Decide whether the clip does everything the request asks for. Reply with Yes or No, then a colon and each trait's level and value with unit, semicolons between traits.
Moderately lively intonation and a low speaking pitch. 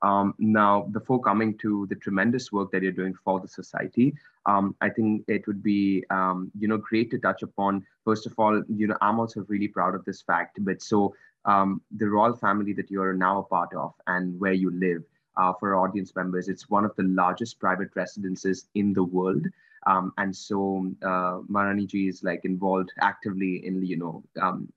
No: narrow, 1.9 semitones; low, 100 Hz